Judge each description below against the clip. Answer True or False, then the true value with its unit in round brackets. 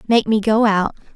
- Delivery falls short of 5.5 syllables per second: True (4.9 syllables/s)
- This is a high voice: True (215 Hz)